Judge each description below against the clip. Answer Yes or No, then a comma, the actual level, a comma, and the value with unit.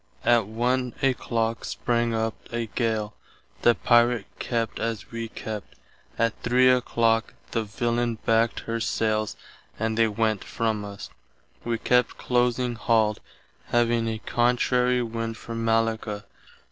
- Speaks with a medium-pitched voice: No, low, 115 Hz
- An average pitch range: No, narrow, 1.1 semitones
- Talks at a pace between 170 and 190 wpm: No, slow, 135 wpm